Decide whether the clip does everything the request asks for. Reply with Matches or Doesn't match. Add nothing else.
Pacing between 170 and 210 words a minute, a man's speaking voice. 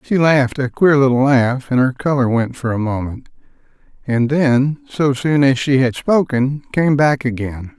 Matches